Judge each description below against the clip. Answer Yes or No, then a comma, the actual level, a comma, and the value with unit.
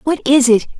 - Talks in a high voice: Yes, very high, 265 Hz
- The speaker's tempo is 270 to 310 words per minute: No, fast, 225 wpm